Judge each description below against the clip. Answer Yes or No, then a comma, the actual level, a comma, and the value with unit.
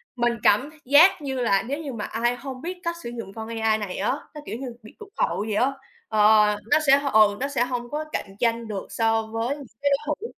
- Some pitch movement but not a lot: Yes, average, 4.4 semitones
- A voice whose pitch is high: Yes, high, 240 Hz